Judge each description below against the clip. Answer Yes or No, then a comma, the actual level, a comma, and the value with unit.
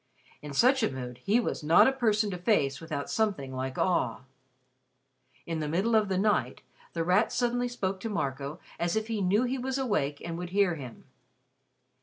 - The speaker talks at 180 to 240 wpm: Yes, average, 195 wpm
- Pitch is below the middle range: No, medium, 185 Hz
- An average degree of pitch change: No, wide, 6.8 semitones